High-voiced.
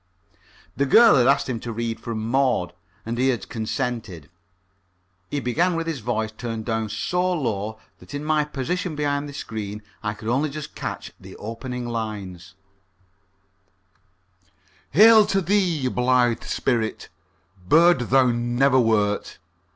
No: low, 125 Hz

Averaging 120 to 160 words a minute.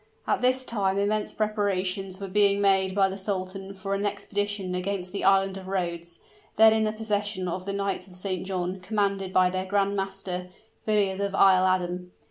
No: average, 185 wpm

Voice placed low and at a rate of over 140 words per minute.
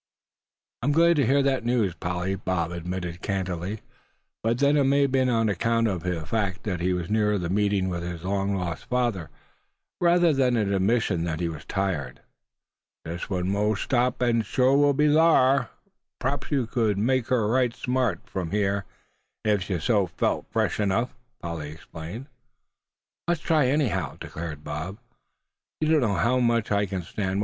Yes: low, 105 Hz; average, 175 wpm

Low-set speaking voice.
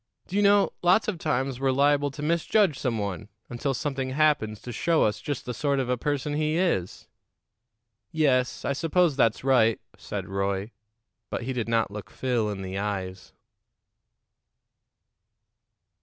Yes: low, 130 Hz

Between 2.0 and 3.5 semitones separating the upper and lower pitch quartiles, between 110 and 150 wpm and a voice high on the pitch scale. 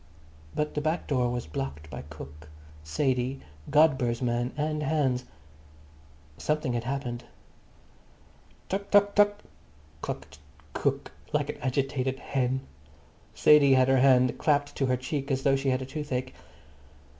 No: average, 3.0 semitones; slow, 135 wpm; low, 135 Hz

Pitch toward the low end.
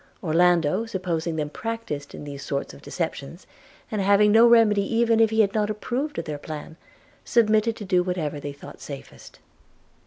No: medium, 185 Hz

